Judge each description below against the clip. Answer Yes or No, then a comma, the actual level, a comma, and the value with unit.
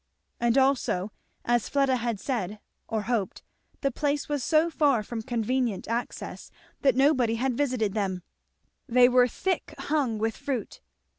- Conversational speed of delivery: Yes, average, 145 wpm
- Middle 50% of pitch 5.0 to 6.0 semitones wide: No, average, 3.6 semitones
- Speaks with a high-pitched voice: Yes, high, 245 Hz